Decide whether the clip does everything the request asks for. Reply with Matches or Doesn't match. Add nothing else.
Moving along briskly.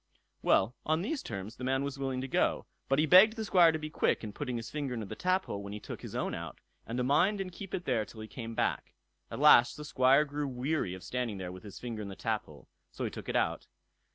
Matches